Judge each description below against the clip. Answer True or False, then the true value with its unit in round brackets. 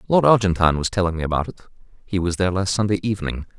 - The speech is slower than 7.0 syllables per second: False (7.8 syllables/s)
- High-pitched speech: False (95 Hz)